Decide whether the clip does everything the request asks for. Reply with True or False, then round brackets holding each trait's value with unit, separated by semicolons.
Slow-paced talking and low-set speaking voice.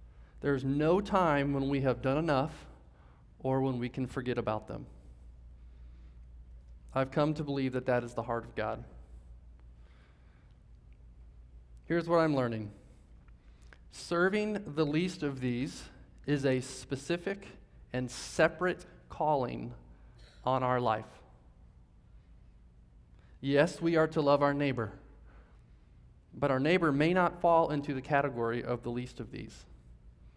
True (130 wpm; 120 Hz)